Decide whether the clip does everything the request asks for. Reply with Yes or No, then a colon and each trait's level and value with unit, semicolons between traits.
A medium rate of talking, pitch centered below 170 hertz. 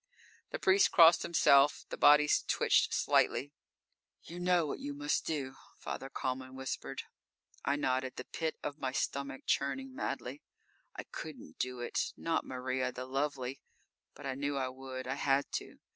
Yes: average, 160 wpm; medium, 140 Hz